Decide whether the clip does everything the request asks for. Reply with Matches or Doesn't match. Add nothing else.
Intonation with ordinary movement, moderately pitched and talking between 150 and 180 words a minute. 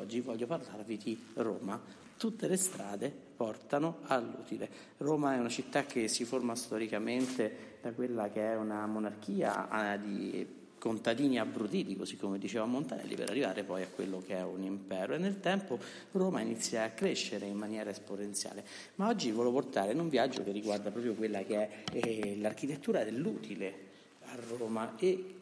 Doesn't match